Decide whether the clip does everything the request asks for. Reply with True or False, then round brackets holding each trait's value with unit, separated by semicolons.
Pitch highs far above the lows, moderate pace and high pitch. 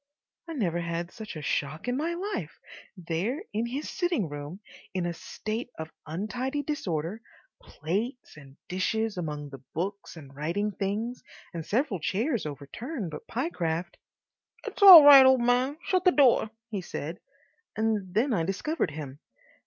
True (7.7 semitones; 155 wpm; 205 Hz)